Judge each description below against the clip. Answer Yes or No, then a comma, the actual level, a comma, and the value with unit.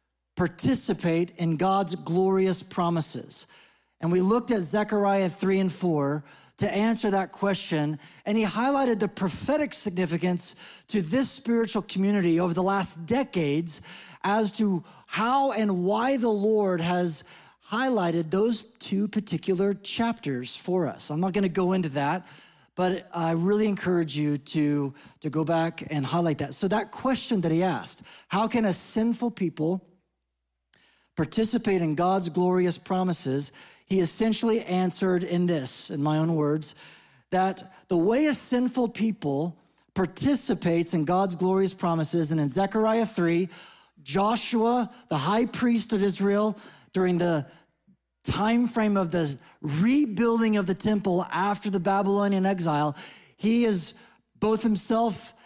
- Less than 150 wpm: Yes, average, 140 wpm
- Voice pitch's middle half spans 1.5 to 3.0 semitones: No, average, 4.1 semitones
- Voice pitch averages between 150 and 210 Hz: Yes, high, 190 Hz